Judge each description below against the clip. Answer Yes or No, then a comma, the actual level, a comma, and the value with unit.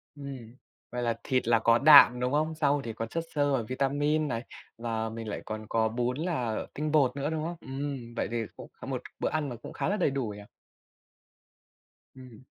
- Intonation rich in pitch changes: No, average, 4.0 semitones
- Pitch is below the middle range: Yes, low, 130 Hz